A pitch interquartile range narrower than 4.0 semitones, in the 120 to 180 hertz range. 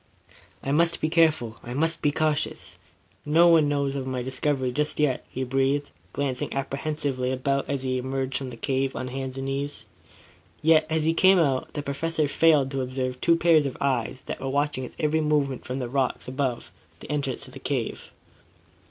Yes: narrow, 2.6 semitones; medium, 140 Hz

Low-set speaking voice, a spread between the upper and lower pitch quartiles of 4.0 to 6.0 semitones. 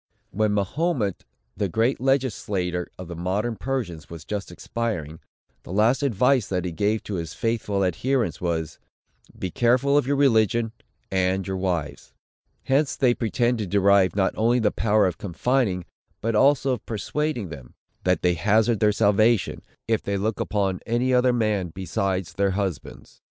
Yes: low, 105 Hz; average, 4.5 semitones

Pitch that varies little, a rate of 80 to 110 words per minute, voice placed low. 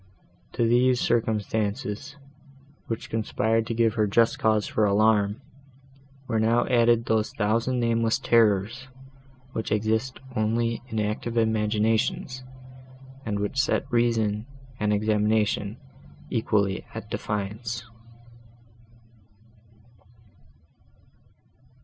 Yes: narrow, 1.8 semitones; slow, 95 wpm; low, 110 Hz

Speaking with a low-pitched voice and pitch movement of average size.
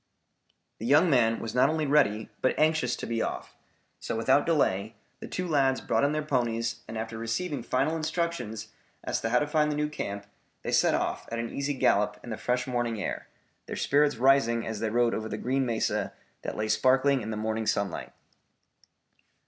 Yes: low, 125 Hz; average, 4.5 semitones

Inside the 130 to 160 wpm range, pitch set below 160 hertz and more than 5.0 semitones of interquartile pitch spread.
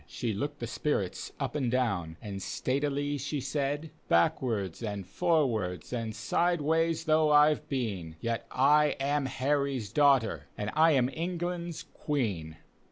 Yes: average, 145 wpm; low, 135 Hz; wide, 5.5 semitones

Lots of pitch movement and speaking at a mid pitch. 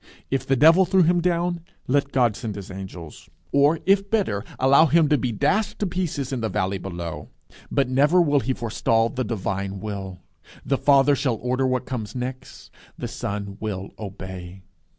No: wide, 6.5 semitones; low, 125 Hz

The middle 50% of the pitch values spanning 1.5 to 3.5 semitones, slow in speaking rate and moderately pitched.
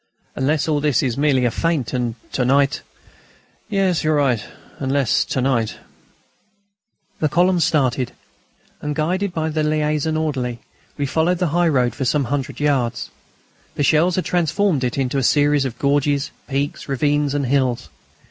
No: average, 3.1 semitones; average, 165 wpm; medium, 145 Hz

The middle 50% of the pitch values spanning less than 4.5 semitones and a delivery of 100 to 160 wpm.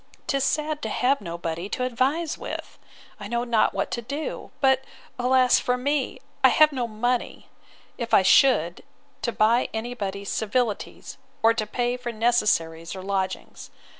Yes: average, 3.8 semitones; average, 155 wpm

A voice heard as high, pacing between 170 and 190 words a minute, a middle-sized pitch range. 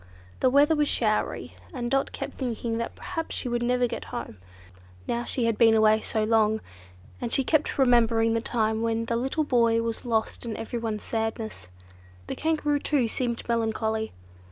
No: high, 235 Hz; average, 175 wpm; narrow, 2.2 semitones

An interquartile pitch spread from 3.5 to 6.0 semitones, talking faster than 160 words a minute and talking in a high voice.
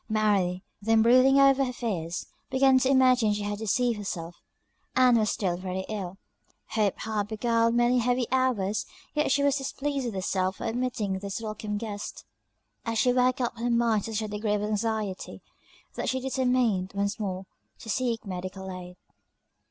Yes: average, 3.9 semitones; average, 170 wpm; high, 220 Hz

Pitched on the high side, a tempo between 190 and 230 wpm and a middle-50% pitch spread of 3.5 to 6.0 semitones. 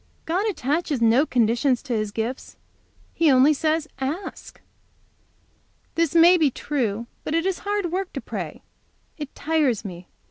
No: very high, 295 Hz; average, 145 wpm; wide, 5.5 semitones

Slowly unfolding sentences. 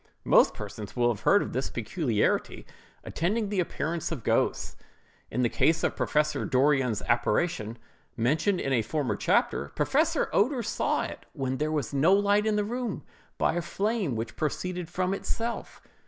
No: average, 165 wpm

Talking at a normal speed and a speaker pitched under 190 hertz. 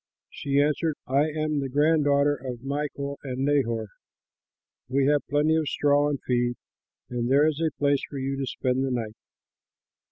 Yes: average, 170 wpm; medium, 140 Hz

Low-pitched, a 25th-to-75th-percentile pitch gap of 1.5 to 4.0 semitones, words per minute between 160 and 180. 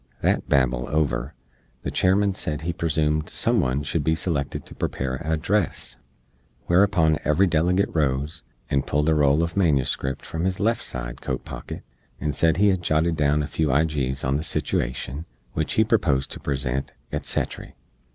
Yes: very low, 75 Hz; average, 3.4 semitones; average, 170 wpm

